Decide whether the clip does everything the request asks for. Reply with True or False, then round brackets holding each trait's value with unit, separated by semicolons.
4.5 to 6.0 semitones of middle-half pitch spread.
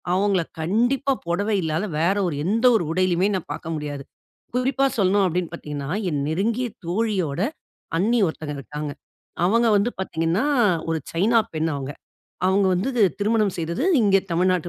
True (4.8 semitones)